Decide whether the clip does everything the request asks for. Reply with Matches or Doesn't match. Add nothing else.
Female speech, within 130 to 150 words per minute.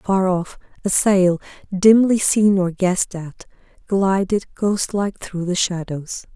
Matches